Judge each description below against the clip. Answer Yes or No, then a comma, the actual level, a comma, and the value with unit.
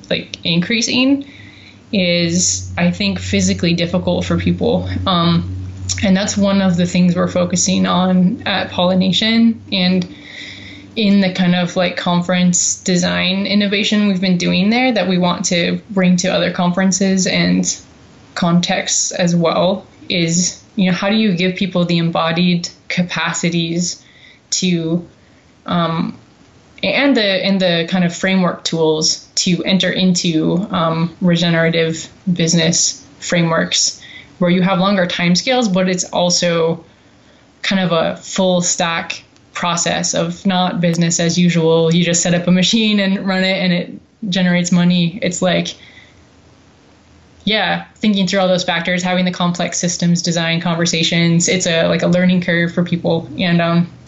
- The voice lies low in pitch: No, medium, 180 Hz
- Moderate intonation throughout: No, narrow, 1.9 semitones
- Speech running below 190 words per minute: Yes, average, 145 wpm